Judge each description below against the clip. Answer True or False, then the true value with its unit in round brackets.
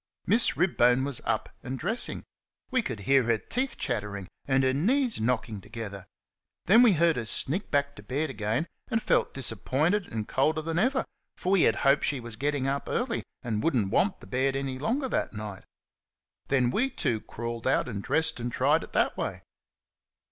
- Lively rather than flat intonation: True (6.6 semitones)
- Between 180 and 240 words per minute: True (190 wpm)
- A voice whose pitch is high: False (135 Hz)